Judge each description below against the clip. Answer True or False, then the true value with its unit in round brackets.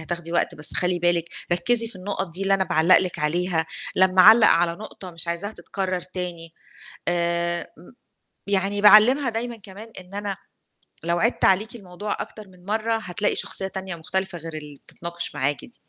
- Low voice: False (185 Hz)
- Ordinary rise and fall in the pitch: True (3.0 semitones)